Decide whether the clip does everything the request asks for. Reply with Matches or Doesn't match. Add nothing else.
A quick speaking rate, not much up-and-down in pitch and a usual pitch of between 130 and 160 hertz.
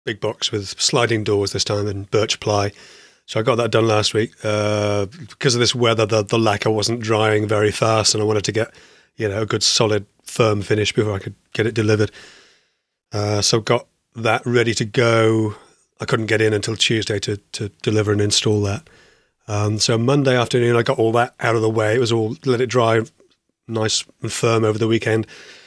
Doesn't match